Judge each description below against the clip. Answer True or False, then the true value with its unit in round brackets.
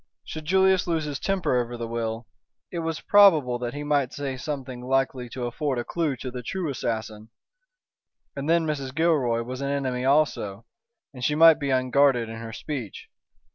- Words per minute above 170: True (180 wpm)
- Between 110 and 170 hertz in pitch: True (135 Hz)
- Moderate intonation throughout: True (4.0 semitones)